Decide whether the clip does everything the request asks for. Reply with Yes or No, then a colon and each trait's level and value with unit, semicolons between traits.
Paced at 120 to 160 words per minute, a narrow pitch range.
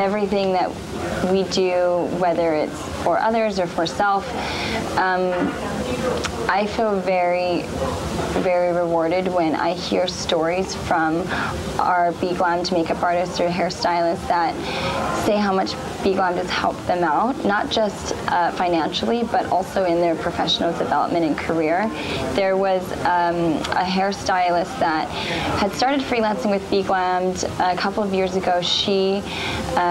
Yes: average, 140 wpm; narrow, 1.9 semitones